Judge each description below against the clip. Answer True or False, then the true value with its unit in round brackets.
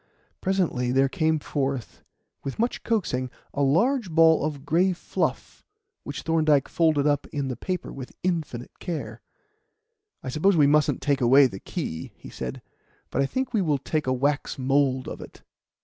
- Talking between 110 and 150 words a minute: False (165 wpm)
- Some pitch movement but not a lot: True (3.7 semitones)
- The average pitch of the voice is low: False (145 Hz)